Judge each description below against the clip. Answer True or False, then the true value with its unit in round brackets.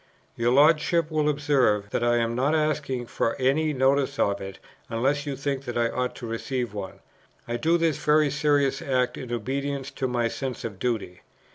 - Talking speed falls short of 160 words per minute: False (185 wpm)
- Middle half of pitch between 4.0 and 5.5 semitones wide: False (3.4 semitones)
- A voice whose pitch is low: True (130 Hz)